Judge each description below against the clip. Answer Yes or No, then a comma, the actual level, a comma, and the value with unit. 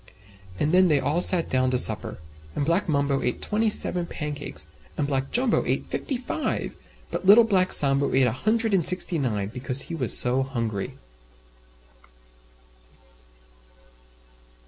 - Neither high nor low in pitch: Yes, medium, 145 Hz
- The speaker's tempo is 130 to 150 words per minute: Yes, average, 145 wpm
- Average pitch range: No, wide, 6.1 semitones